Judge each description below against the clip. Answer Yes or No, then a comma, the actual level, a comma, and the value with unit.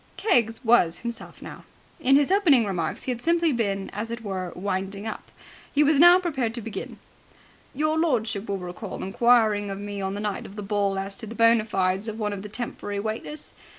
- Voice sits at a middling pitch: No, high, 220 Hz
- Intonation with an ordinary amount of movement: Yes, average, 3.7 semitones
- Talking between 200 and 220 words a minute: Yes, fast, 205 wpm